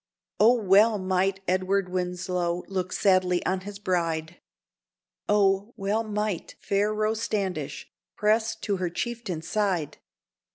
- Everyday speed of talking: No, slow, 120 wpm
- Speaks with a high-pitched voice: Yes, high, 195 Hz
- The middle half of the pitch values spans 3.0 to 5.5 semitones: No, narrow, 2.6 semitones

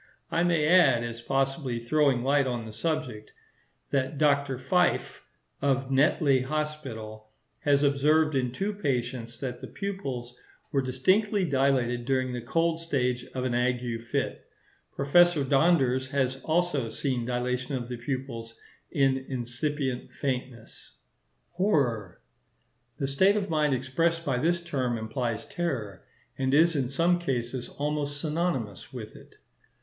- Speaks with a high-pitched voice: No, low, 135 Hz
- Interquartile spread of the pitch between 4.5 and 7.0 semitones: No, average, 3.8 semitones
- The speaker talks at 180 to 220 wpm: No, slow, 135 wpm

